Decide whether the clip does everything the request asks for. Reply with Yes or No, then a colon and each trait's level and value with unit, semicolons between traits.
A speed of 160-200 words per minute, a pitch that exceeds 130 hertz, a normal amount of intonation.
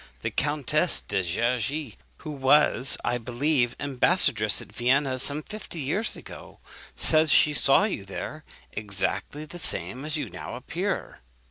No: average, 140 wpm; medium, 140 Hz; average, 4.1 semitones